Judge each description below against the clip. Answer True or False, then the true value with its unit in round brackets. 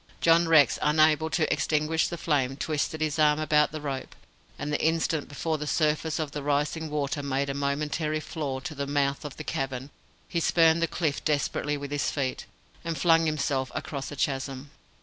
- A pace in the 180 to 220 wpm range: True (190 wpm)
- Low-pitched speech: False (150 Hz)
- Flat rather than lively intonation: True (2.0 semitones)